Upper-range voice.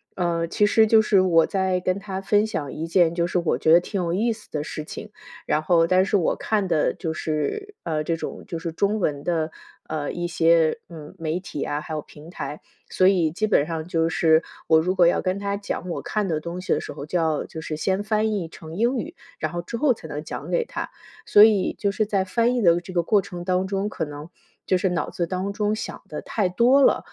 No: medium, 180 Hz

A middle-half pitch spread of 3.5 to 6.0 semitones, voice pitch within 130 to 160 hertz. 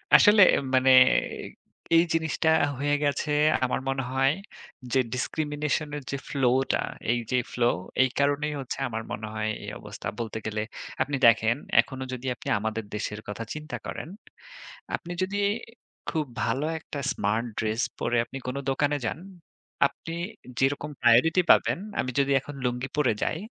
Yes: average, 3.9 semitones; low, 135 Hz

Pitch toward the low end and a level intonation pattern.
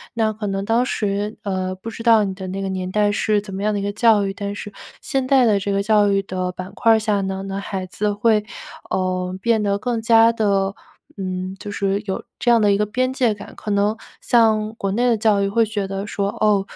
No: high, 205 Hz; narrow, 2.1 semitones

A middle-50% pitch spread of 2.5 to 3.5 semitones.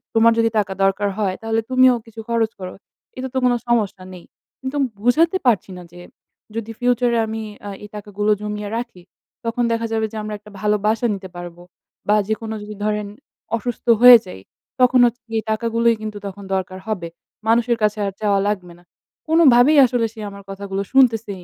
Yes: average, 2.8 semitones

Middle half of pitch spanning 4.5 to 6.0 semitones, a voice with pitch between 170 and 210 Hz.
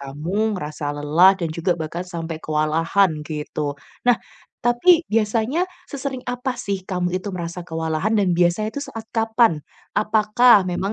Yes: wide, 5.5 semitones; high, 190 Hz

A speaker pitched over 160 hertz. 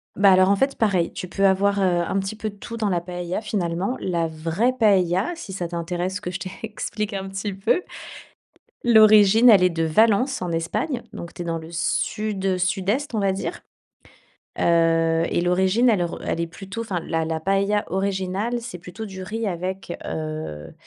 Yes: high, 190 Hz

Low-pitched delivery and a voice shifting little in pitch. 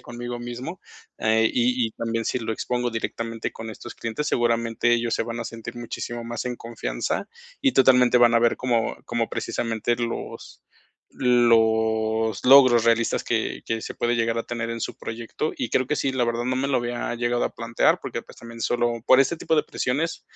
Yes: low, 120 Hz; narrow, 1.2 semitones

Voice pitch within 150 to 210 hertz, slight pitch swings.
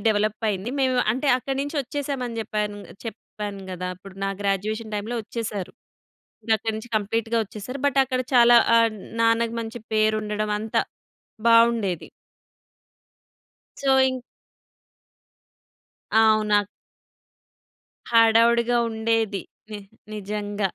No: high, 220 Hz; narrow, 2.1 semitones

